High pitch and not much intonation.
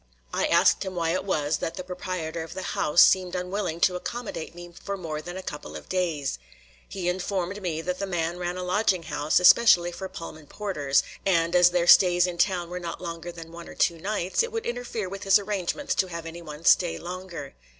No: medium, 180 Hz; narrow, 2.1 semitones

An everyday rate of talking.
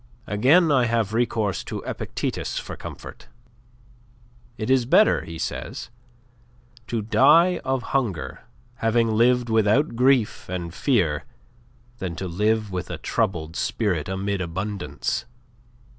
No: slow, 120 wpm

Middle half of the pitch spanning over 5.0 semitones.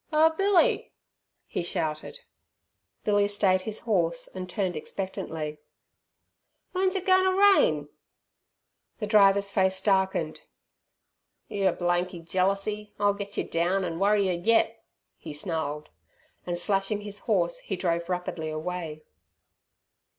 No: average, 3.4 semitones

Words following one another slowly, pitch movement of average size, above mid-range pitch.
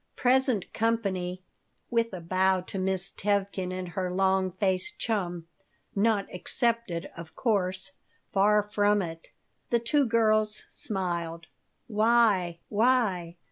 Yes: slow, 115 wpm; average, 3.3 semitones; high, 195 Hz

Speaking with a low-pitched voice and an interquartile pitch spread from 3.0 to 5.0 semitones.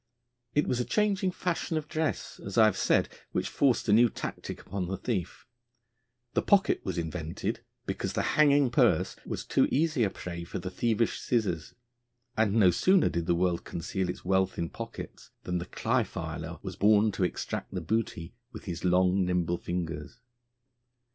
No: very low, 95 Hz; wide, 5.6 semitones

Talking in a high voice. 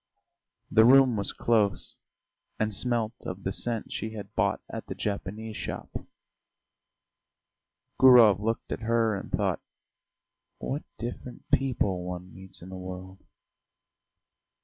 No: low, 110 Hz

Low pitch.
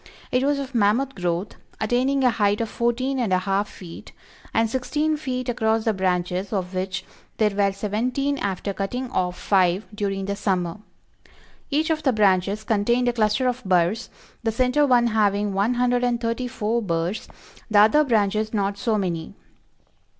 No: high, 215 Hz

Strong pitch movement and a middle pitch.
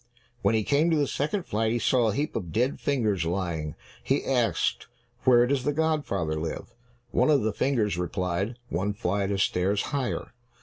No: wide, 6.3 semitones; low, 110 Hz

